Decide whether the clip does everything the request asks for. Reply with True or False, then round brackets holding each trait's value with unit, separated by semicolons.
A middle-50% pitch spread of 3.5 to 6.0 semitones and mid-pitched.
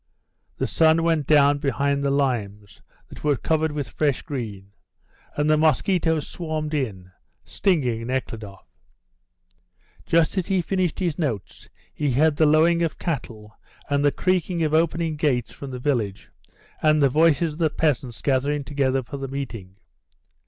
True (3.8 semitones; 145 Hz)